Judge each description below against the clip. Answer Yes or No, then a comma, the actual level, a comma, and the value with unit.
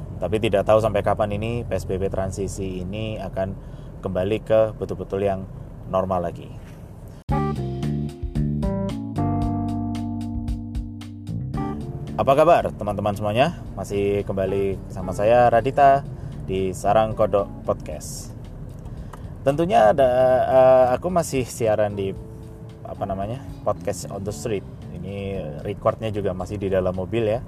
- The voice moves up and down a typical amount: Yes, average, 3.0 semitones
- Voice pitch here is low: Yes, low, 100 Hz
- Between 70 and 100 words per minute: No, average, 110 wpm